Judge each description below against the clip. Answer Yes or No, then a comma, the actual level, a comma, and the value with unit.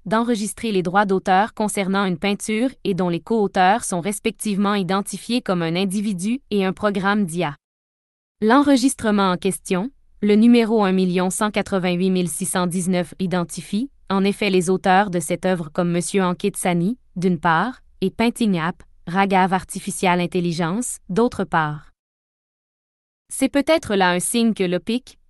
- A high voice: Yes, high, 195 Hz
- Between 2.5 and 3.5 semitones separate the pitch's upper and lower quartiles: Yes, average, 2.8 semitones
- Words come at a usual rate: No, slow, 135 wpm